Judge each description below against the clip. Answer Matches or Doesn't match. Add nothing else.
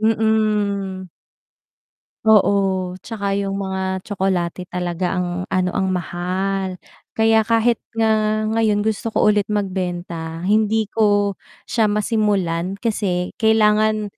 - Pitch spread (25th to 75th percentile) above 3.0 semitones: Doesn't match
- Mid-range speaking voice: Doesn't match